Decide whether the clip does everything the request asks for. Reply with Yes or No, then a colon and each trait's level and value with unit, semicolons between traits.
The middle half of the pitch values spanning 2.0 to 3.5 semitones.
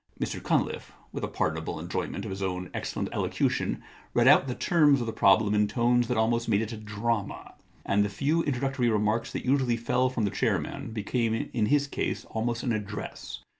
Yes: average, 2.9 semitones